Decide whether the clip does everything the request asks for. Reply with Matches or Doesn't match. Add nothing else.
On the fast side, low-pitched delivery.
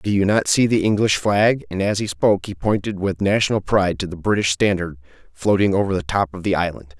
Matches